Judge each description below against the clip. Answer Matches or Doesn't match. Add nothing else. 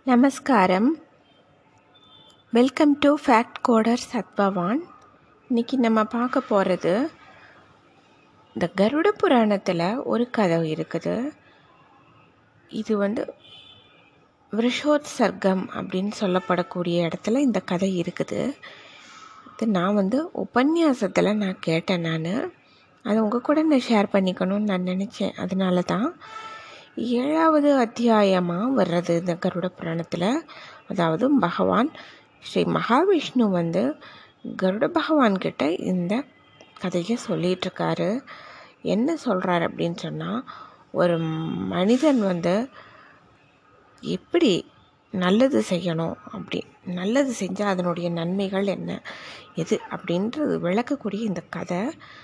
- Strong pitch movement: Matches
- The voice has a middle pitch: Doesn't match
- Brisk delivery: Doesn't match